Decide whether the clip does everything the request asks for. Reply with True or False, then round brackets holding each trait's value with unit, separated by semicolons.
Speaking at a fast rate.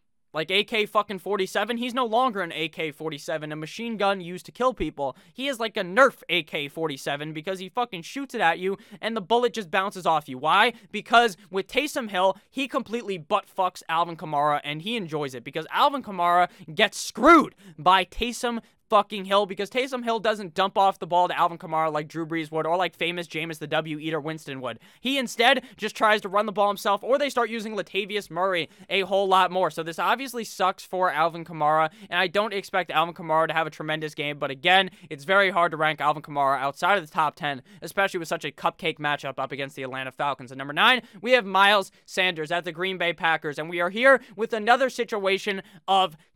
True (215 wpm)